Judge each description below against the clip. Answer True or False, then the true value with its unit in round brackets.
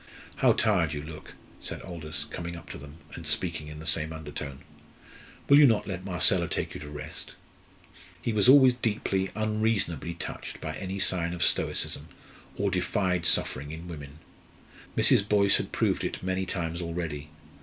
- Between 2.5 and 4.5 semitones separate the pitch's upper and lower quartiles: True (4.0 semitones)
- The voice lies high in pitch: False (85 Hz)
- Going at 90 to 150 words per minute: False (165 wpm)